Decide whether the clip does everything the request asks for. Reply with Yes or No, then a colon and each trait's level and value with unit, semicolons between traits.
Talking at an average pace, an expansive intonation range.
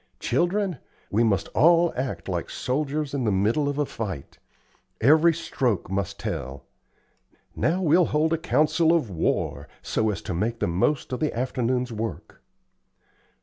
Yes: average, 150 wpm; wide, 6.8 semitones